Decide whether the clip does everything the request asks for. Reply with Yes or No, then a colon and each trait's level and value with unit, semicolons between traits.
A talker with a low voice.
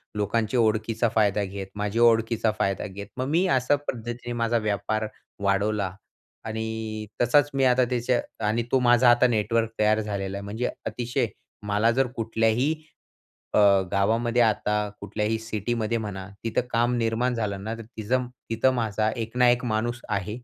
Yes: low, 115 Hz